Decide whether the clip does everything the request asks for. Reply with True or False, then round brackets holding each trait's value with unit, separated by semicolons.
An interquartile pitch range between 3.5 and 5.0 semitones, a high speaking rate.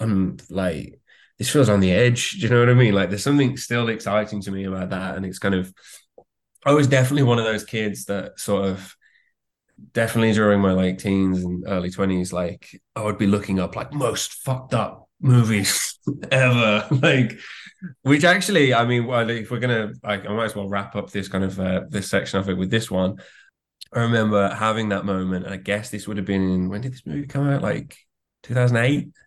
True (3.9 semitones; 215 wpm)